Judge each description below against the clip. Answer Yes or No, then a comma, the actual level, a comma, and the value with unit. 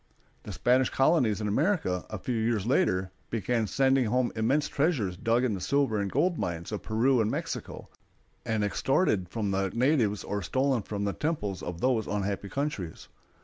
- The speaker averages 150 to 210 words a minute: Yes, average, 175 wpm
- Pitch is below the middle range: Yes, low, 110 Hz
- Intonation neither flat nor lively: Yes, average, 4.9 semitones